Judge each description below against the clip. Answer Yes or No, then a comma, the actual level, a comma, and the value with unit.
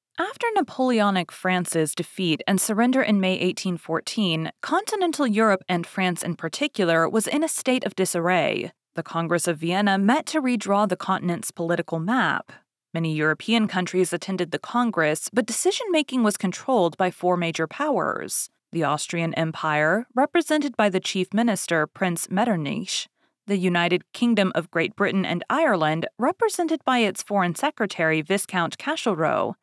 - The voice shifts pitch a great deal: Yes, wide, 6.2 semitones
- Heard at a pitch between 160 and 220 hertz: Yes, high, 190 Hz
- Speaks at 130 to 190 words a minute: Yes, average, 145 wpm